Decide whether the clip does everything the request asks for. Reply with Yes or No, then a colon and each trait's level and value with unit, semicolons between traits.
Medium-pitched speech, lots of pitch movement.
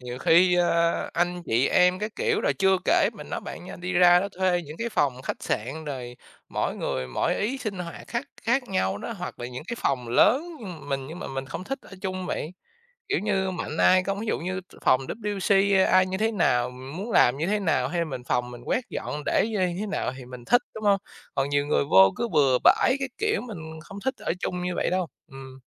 Yes: medium, 180 Hz; wide, 6.8 semitones